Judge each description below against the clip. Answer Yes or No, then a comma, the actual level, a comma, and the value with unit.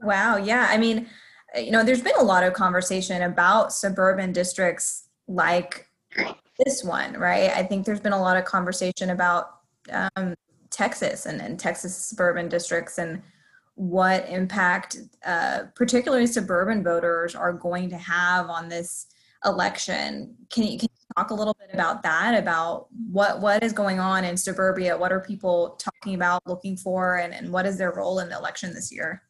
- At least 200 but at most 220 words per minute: No, average, 175 wpm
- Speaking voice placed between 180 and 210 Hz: Yes, medium, 185 Hz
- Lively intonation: No, narrow, 2.6 semitones